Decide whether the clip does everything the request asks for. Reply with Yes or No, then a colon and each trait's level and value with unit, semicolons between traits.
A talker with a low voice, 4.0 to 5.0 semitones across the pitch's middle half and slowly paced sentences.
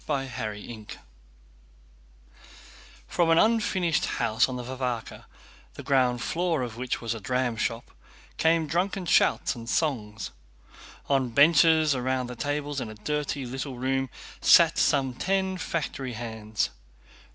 Yes: low, 130 Hz; average, 4.5 semitones; slow, 130 wpm